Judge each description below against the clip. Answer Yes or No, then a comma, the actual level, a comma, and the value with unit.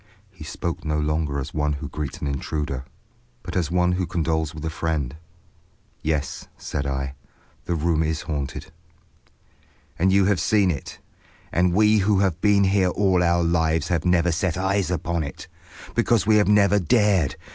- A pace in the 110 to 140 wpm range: No, average, 170 wpm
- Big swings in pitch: No, average, 3.7 semitones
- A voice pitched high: No, very low, 85 Hz